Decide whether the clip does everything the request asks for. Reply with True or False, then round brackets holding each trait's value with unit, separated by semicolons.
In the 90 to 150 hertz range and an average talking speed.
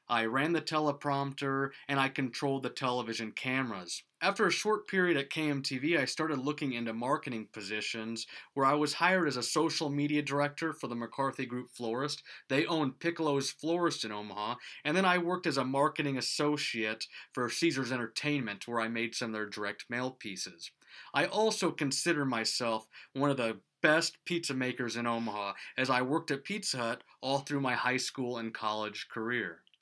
True (135 Hz; 175 wpm)